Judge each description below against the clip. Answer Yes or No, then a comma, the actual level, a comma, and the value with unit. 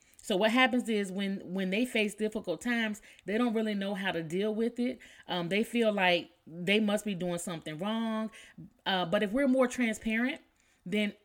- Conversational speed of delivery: Yes, average, 190 wpm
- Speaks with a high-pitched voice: Yes, high, 210 Hz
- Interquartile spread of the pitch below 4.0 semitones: Yes, average, 2.9 semitones